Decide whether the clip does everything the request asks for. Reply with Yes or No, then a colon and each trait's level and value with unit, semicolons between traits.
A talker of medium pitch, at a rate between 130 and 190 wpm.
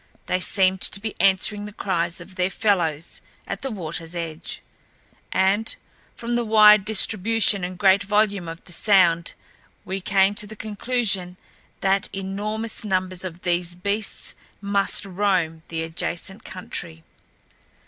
No: high, 195 Hz; average, 140 wpm